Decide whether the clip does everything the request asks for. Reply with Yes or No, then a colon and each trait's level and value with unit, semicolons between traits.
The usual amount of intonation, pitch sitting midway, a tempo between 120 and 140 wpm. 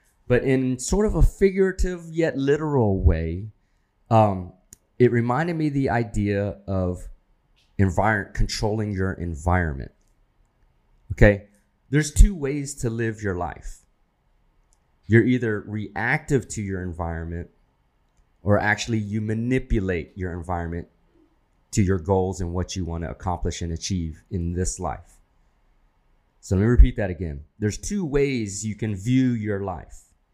No: average, 5.0 semitones; low, 100 Hz; slow, 135 wpm